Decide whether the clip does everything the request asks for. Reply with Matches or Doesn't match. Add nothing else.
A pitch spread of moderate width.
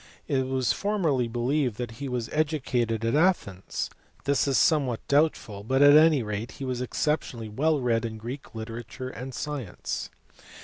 Matches